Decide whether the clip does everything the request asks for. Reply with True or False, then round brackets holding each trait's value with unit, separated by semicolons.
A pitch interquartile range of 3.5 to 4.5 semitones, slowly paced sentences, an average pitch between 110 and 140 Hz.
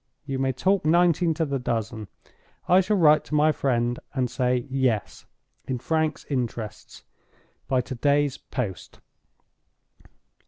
True (4.0 semitones; 125 wpm; 135 Hz)